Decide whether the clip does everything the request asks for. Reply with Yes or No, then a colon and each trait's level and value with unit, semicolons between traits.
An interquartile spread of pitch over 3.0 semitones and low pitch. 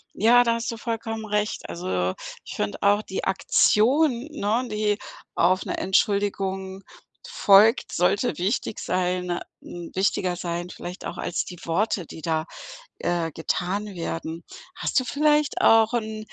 No: average, 4.2 semitones; high, 200 Hz